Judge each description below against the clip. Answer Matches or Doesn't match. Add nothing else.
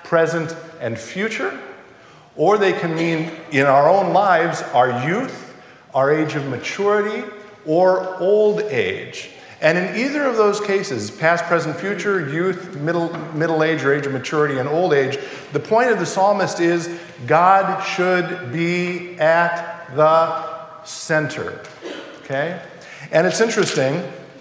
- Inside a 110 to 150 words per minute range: Matches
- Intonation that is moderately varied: Matches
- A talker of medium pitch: Matches